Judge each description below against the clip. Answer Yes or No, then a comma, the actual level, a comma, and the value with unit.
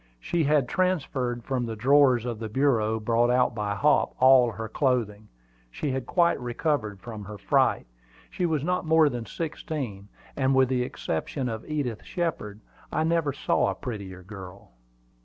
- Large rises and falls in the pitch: No, average, 5.0 semitones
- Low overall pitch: Yes, low, 125 Hz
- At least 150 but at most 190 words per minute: Yes, average, 165 wpm